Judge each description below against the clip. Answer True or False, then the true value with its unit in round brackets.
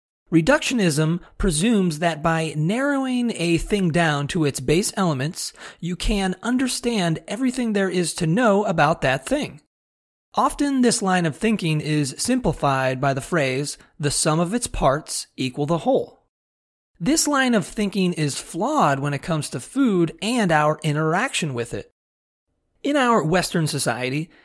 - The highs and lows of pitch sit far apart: True (6.7 semitones)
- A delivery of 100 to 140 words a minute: False (150 wpm)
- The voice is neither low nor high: True (170 Hz)